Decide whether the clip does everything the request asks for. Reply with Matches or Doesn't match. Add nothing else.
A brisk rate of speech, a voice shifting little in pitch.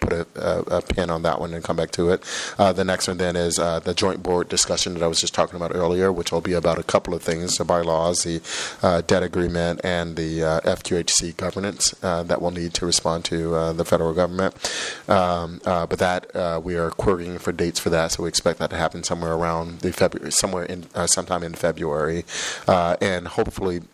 Matches